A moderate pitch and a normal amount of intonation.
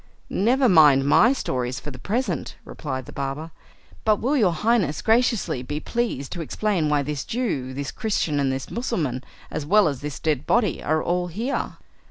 No: medium, 155 Hz; wide, 7.9 semitones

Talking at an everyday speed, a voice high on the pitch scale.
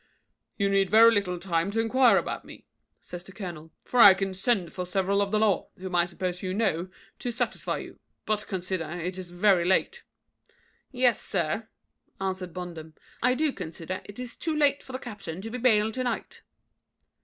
Yes: average, 190 wpm; high, 195 Hz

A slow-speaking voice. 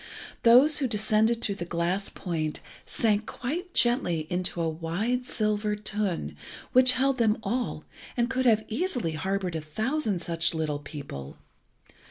No: average, 145 wpm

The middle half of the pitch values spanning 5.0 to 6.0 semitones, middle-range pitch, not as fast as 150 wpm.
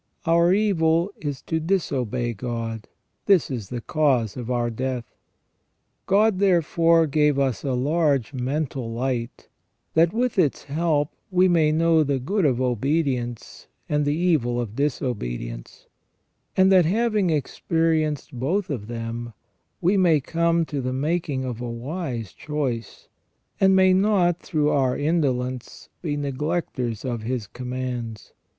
Yes: average, 5.3 semitones; medium, 145 Hz; average, 140 wpm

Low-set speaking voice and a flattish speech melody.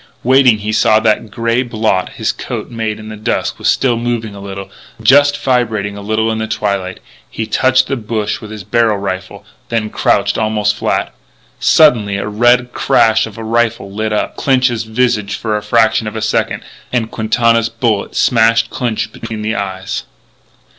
Yes: low, 110 Hz; narrow, 1.9 semitones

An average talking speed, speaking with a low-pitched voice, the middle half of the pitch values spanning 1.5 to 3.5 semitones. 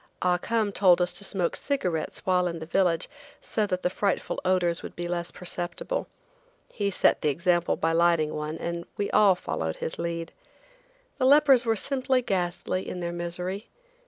No: average, 175 wpm; medium, 180 Hz; average, 2.8 semitones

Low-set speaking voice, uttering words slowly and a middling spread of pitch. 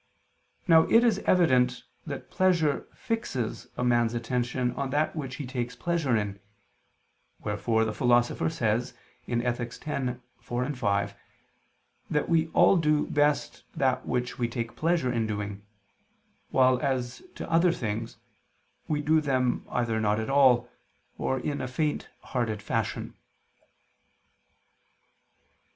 Yes: low, 125 Hz; slow, 130 wpm; average, 3.9 semitones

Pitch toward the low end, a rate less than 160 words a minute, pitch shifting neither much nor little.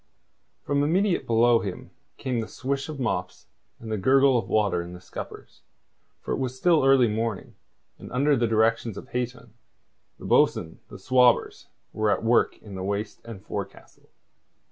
No: low, 115 Hz; average, 165 wpm; average, 3.5 semitones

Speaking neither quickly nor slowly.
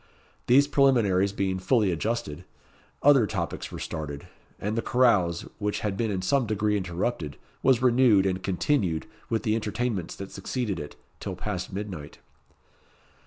Yes: average, 145 wpm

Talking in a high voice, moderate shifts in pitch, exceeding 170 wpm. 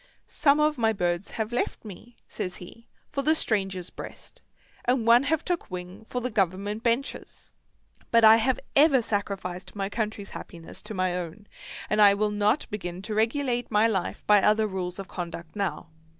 Yes: high, 210 Hz; average, 3.9 semitones; average, 180 wpm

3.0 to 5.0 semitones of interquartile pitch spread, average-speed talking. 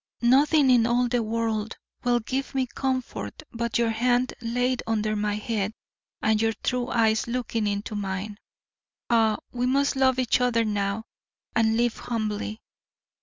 No: narrow, 2.4 semitones; average, 150 wpm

